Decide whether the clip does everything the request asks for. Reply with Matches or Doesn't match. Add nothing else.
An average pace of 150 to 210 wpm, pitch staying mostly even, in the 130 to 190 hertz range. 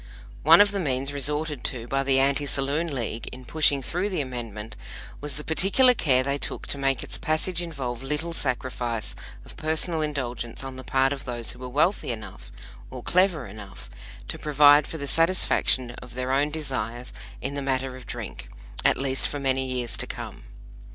Doesn't match